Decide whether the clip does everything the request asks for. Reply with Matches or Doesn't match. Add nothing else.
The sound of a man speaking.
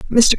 Doesn't match